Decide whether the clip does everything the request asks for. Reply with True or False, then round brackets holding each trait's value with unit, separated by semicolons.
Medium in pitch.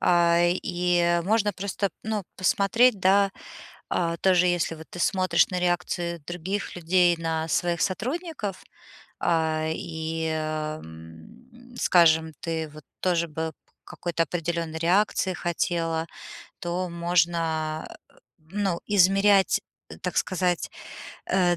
True (175 Hz)